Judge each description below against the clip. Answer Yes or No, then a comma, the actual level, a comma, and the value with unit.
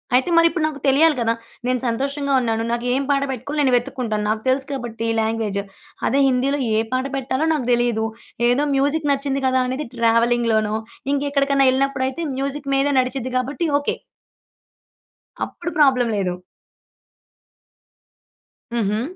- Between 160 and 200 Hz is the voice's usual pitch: No, very high, 260 Hz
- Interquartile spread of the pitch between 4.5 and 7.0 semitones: No, average, 2.9 semitones